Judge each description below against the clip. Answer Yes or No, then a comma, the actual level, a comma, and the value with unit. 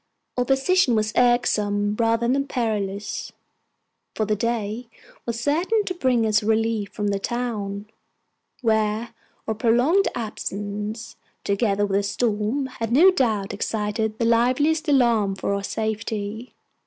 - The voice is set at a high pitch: Yes, high, 225 Hz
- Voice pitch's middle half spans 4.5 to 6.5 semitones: No, average, 2.9 semitones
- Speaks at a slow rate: Yes, slow, 130 wpm